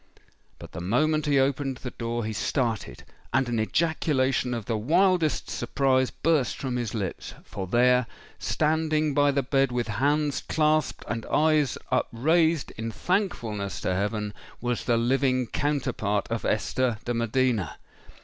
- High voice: No, low, 130 Hz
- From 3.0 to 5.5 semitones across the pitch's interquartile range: Yes, average, 4.5 semitones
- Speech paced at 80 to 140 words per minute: Yes, slow, 135 wpm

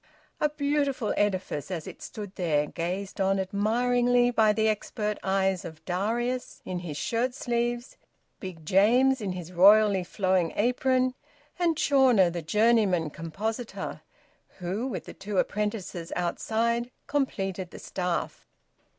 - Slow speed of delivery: Yes, slow, 130 wpm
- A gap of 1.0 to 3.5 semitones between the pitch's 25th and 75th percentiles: No, average, 4.8 semitones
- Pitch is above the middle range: Yes, high, 205 Hz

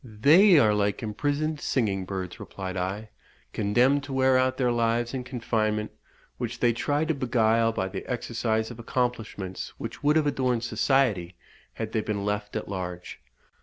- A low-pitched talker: Yes, low, 115 Hz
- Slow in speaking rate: No, average, 165 wpm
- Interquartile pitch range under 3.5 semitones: No, average, 4.0 semitones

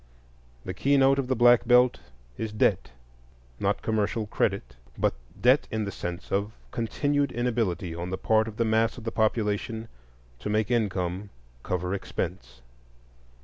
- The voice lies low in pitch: Yes, low, 110 Hz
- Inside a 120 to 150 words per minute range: Yes, average, 145 wpm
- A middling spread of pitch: Yes, average, 3.6 semitones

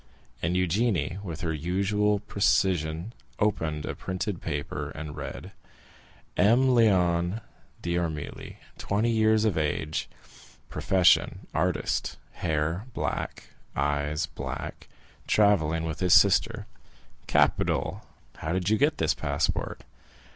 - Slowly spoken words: Yes, slow, 105 wpm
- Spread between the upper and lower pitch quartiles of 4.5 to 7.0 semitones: Yes, average, 4.9 semitones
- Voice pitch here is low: Yes, very low, 90 Hz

